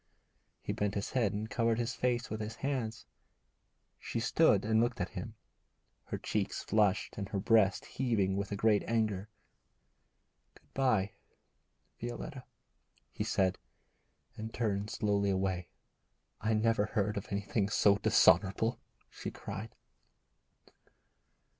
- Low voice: Yes, low, 105 Hz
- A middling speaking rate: No, slow, 130 wpm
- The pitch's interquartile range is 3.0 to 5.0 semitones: No, narrow, 2.4 semitones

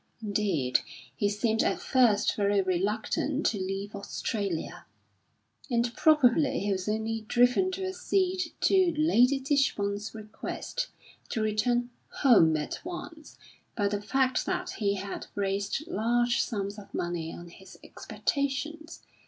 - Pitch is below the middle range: No, high, 220 Hz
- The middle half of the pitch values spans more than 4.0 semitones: Yes, wide, 5.4 semitones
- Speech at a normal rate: No, slow, 130 wpm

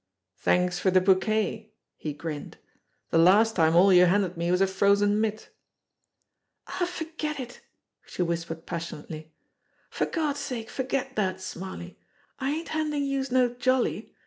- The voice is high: Yes, high, 205 Hz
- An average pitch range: No, wide, 6.7 semitones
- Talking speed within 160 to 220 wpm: No, average, 150 wpm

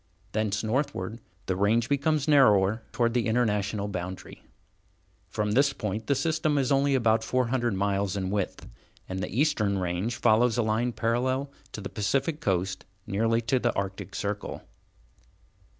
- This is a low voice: Yes, low, 110 Hz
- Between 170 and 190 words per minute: No, average, 150 wpm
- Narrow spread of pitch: No, average, 4.3 semitones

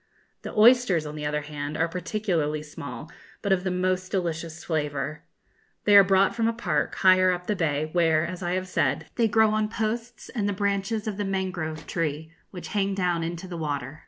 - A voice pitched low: No, medium, 180 Hz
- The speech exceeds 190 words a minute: Yes, average, 200 wpm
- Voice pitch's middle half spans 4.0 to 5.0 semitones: Yes, average, 4.3 semitones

